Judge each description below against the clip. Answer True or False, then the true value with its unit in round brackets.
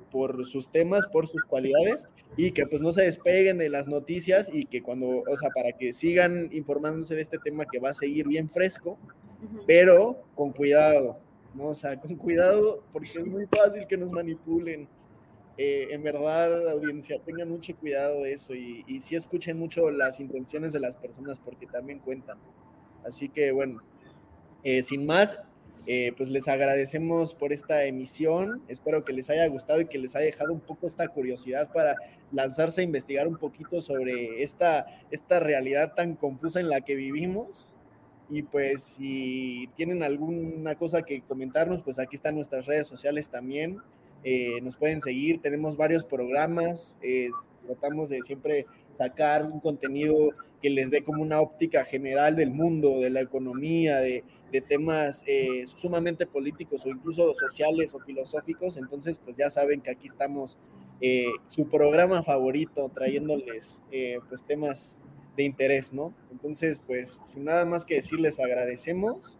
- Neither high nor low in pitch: True (150 Hz)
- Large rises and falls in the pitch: False (3.5 semitones)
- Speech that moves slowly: False (165 wpm)